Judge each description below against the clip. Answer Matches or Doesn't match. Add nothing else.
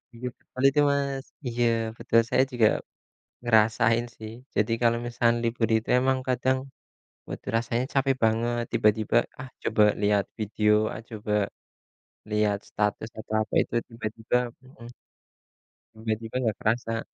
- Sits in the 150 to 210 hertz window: Doesn't match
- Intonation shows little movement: Matches